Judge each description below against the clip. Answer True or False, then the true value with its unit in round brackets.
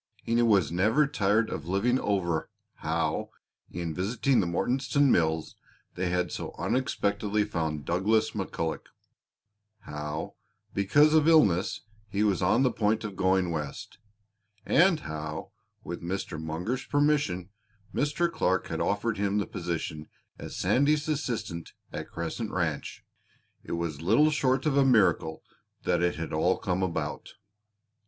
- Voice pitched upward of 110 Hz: False (100 Hz)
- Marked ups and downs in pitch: True (6.5 semitones)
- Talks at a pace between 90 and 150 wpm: True (140 wpm)